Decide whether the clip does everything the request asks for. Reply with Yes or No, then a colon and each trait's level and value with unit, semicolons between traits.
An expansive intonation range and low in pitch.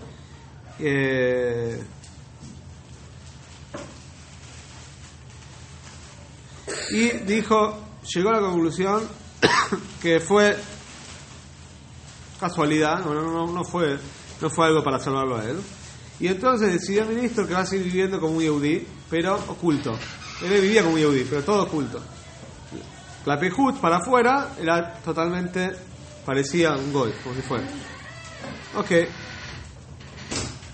No: wide, 5.7 semitones; medium, 165 Hz